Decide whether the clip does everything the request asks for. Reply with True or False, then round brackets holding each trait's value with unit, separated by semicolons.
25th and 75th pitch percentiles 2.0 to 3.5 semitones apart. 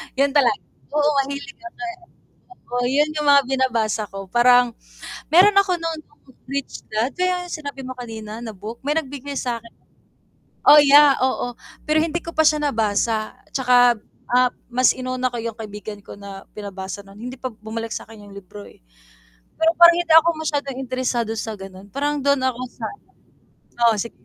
False (4.8 semitones)